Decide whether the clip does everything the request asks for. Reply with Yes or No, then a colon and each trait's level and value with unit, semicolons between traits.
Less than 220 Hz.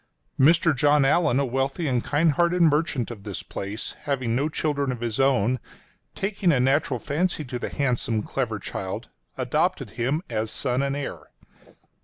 Yes: low, 135 Hz